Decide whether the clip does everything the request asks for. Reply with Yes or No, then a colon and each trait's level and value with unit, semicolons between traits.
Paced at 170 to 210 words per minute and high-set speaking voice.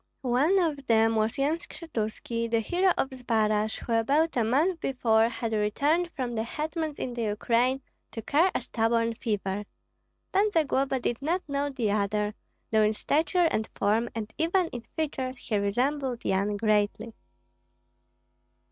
No: average, 155 wpm; high, 240 Hz